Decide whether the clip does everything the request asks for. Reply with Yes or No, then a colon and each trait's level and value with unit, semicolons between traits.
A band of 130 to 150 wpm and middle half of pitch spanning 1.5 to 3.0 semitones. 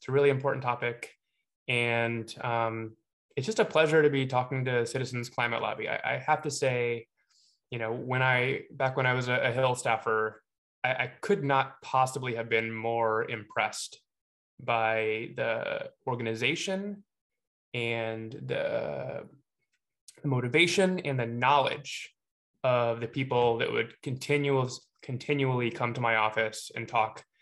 Yes: average, 145 wpm; average, 2.7 semitones